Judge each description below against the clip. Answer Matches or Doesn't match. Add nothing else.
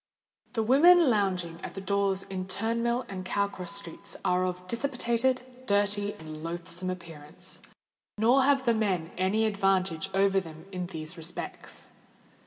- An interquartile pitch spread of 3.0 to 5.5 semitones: Matches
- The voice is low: Doesn't match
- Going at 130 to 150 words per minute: Matches